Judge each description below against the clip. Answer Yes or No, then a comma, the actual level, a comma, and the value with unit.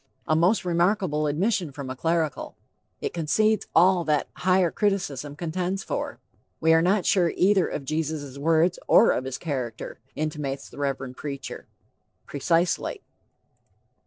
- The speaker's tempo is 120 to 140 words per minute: Yes, slow, 135 wpm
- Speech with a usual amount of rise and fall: Yes, average, 4.1 semitones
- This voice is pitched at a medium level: Yes, medium, 160 Hz